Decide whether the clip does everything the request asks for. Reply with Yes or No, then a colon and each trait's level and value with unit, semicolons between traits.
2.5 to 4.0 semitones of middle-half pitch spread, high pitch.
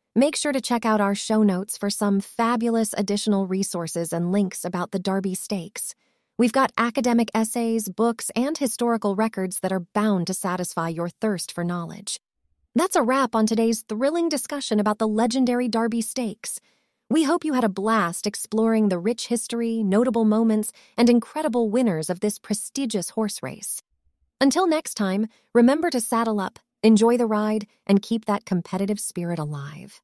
Yes: average, 3.3 semitones; high, 220 Hz